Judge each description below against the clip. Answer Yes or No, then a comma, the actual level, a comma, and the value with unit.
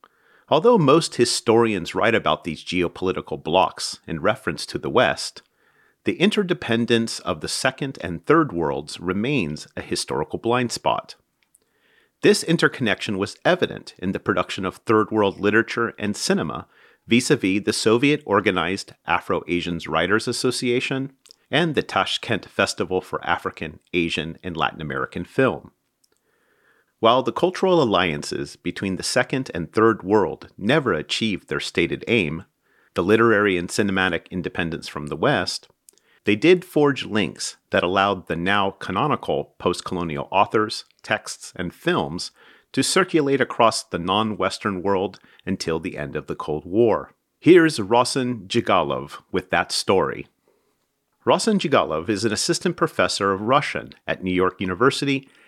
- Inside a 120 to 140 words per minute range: Yes, slow, 135 wpm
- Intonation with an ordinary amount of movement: No, wide, 6.6 semitones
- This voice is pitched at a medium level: No, low, 110 Hz